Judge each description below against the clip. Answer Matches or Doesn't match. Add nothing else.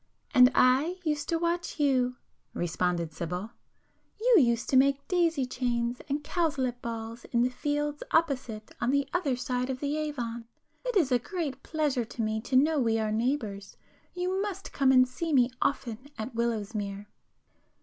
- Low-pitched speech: Doesn't match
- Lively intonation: Doesn't match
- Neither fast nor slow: Matches